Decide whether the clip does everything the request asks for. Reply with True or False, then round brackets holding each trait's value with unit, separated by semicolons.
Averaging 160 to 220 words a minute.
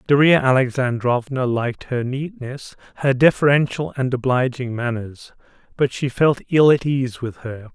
False (140 wpm)